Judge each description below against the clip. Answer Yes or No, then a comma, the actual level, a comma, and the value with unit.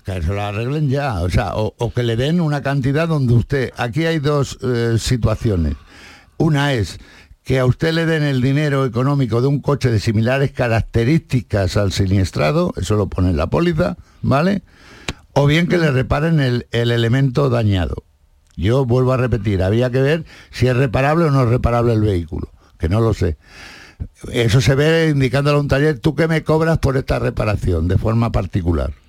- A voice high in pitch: No, low, 125 Hz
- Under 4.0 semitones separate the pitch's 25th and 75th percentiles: No, wide, 5.4 semitones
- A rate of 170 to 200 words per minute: Yes, fast, 190 wpm